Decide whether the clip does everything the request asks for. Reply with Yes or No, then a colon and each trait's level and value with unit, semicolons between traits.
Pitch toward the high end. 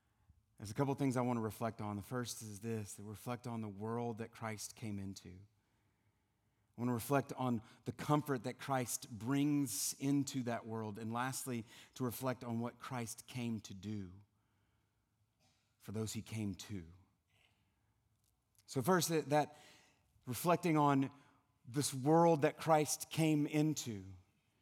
No: low, 115 Hz